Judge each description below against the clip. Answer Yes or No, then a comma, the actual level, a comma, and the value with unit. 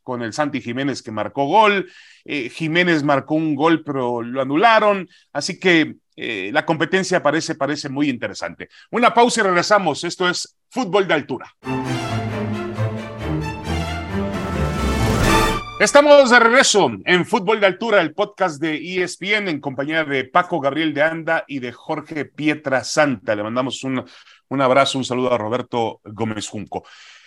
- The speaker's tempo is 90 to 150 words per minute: Yes, average, 145 wpm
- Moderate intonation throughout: No, wide, 7.0 semitones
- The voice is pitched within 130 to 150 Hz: Yes, medium, 145 Hz